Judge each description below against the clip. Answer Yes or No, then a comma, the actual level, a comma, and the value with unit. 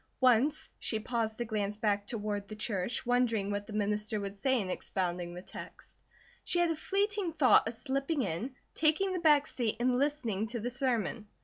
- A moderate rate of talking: Yes, average, 190 wpm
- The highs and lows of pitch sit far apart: No, average, 4.9 semitones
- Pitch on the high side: Yes, high, 230 Hz